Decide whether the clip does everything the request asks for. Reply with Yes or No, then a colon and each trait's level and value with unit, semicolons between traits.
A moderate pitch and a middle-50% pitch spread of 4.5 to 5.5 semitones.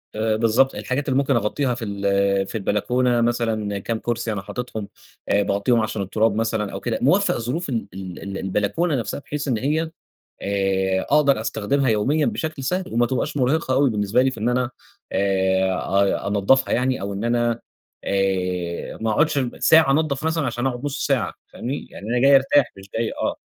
No: low, 115 Hz; average, 4.9 semitones